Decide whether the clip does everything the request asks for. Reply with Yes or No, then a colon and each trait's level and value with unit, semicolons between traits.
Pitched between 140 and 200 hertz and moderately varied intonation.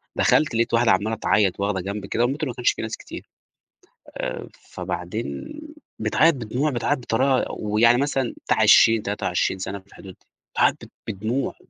No: low, 115 Hz; average, 3.9 semitones